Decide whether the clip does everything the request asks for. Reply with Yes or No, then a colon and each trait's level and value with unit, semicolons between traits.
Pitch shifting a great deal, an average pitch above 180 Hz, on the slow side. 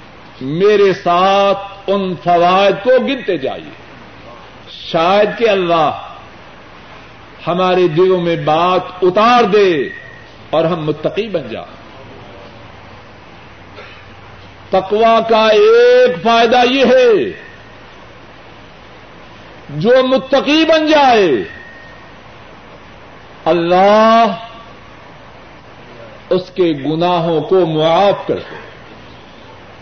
Yes: wide, 6.3 semitones; high, 190 Hz; slow, 75 wpm